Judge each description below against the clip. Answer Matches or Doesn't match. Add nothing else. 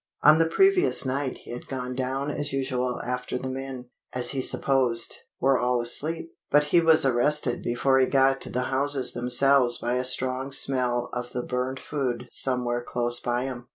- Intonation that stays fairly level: Matches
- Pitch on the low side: Matches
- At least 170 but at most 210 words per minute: Matches